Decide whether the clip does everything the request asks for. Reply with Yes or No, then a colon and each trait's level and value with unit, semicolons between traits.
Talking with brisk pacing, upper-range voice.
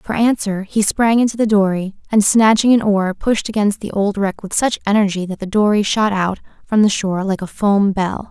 Yes: fast, 225 wpm; high, 205 Hz